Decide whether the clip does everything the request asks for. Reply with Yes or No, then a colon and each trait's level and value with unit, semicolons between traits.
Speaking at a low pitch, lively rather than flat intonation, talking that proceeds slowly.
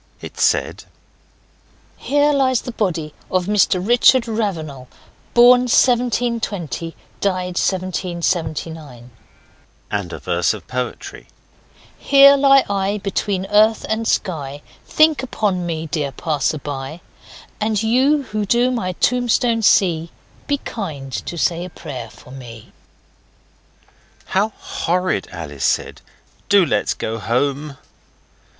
No: medium, 185 Hz; wide, 7.4 semitones; slow, 115 wpm